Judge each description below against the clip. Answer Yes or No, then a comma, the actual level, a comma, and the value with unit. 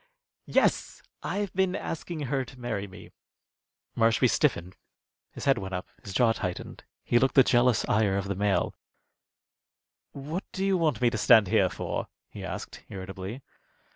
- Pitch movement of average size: No, wide, 6.0 semitones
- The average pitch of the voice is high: No, low, 120 Hz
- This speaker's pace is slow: No, average, 160 wpm